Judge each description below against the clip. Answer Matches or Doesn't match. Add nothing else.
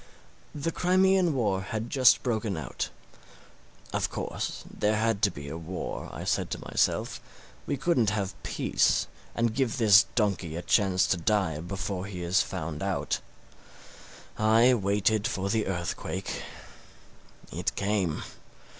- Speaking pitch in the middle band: Doesn't match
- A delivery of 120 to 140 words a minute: Matches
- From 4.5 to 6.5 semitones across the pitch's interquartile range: Doesn't match